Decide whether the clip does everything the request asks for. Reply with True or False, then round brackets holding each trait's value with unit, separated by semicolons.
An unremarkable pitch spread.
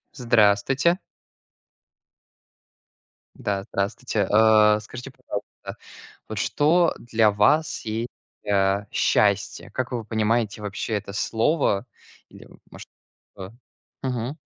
True (3.3 semitones)